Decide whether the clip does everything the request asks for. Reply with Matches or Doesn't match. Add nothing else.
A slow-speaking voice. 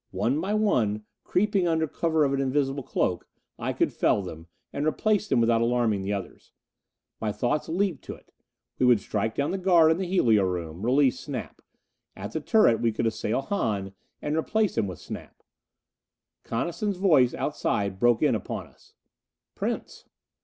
Doesn't match